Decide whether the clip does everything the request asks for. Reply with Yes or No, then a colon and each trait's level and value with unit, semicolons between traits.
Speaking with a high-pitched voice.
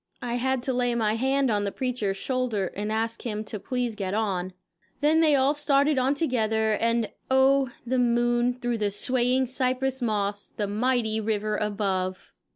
Yes: high, 240 Hz